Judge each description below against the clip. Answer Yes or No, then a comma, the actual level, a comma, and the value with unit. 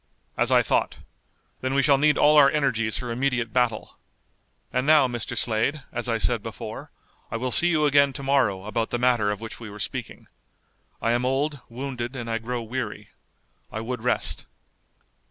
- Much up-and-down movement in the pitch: No, average, 3.3 semitones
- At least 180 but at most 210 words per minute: Yes, average, 185 wpm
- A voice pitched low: Yes, low, 125 Hz